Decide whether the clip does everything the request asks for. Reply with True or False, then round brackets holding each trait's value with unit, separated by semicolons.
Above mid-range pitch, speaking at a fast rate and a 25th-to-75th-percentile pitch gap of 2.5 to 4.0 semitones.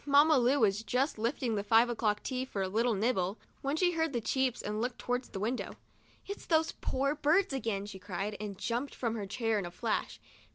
False (235 Hz; 220 wpm; 4.5 semitones)